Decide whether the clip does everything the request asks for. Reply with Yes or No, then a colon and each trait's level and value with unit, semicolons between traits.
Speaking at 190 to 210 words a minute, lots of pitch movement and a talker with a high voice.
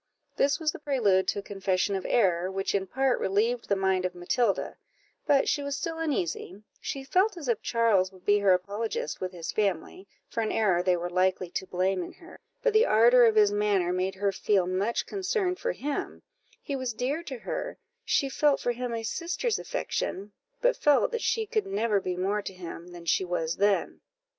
Yes: fast, 205 wpm; wide, 6.9 semitones; high, 210 Hz